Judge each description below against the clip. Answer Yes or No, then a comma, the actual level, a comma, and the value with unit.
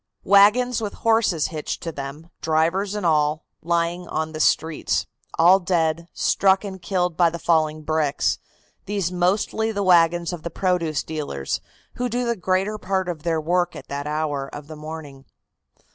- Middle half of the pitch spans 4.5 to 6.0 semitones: No, average, 3.4 semitones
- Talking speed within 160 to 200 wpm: Yes, average, 165 wpm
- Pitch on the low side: No, medium, 170 Hz